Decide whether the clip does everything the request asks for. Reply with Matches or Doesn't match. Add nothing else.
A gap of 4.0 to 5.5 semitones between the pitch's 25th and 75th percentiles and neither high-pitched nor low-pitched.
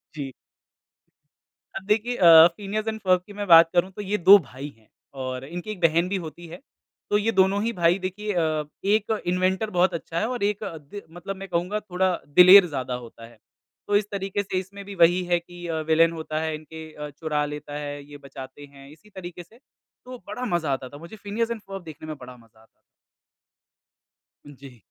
Matches